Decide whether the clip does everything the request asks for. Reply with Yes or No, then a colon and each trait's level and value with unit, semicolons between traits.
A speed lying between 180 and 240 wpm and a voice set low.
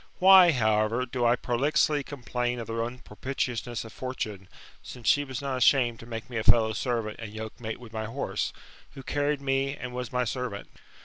Yes: average, 185 wpm; low, 120 Hz